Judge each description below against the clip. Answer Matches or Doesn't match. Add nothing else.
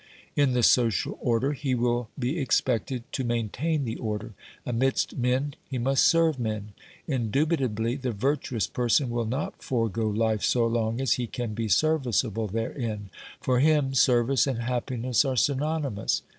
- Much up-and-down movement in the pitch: Doesn't match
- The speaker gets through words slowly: Doesn't match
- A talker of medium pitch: Doesn't match